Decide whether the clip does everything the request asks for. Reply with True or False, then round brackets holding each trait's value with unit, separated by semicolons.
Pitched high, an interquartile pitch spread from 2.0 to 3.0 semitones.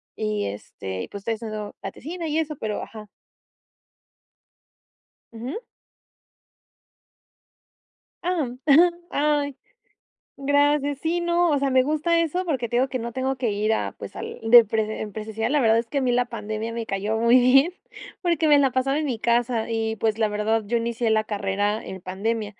False (235 Hz; 4.7 semitones)